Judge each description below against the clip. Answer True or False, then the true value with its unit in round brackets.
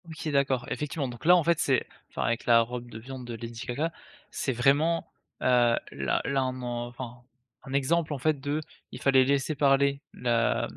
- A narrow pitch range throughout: False (3.0 semitones)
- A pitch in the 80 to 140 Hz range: True (135 Hz)